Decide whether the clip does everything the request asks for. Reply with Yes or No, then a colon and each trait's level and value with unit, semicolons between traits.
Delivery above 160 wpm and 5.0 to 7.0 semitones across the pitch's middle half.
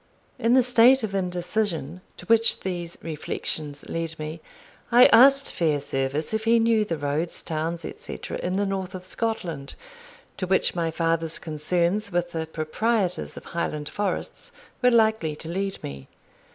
No: average, 150 wpm; average, 5.3 semitones